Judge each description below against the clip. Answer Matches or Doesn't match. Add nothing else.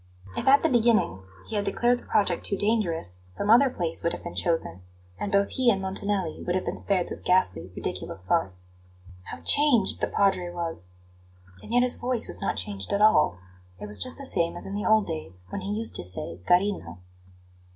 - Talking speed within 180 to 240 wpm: Matches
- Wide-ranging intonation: Matches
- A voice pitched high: Matches